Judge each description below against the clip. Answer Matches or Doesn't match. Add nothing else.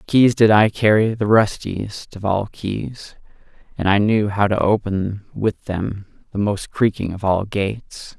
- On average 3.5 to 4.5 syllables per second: Matches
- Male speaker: Matches